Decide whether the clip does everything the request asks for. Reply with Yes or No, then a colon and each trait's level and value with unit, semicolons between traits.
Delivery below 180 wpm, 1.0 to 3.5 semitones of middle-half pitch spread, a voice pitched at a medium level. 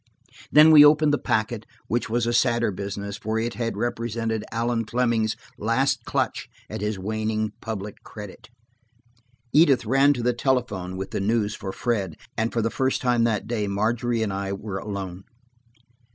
No: average, 165 wpm; average, 2.7 semitones; low, 110 Hz